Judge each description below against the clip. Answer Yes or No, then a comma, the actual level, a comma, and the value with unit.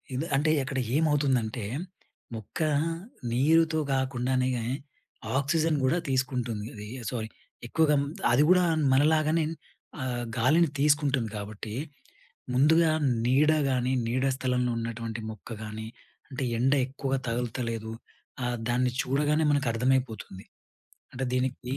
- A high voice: No, low, 130 Hz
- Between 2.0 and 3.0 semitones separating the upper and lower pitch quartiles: No, average, 3.5 semitones